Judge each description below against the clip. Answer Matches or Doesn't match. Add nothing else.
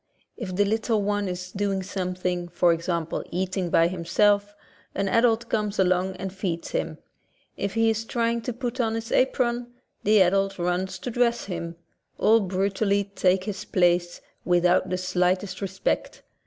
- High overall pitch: Matches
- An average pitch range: Matches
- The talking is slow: Doesn't match